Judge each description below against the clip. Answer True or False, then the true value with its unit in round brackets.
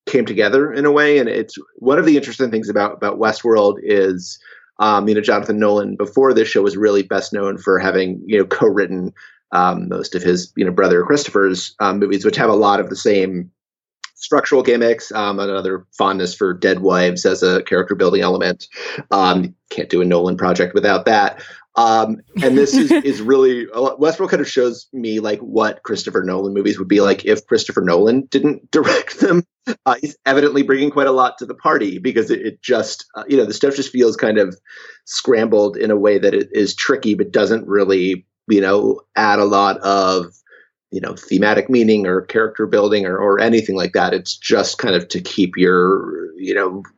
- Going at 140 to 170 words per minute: False (205 wpm)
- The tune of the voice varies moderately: False (5.9 semitones)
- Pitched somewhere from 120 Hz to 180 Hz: False (105 Hz)